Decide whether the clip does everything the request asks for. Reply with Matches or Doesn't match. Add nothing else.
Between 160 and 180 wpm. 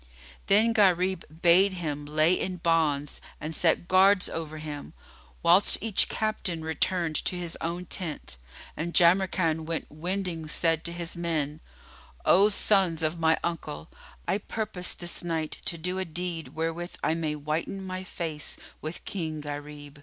Doesn't match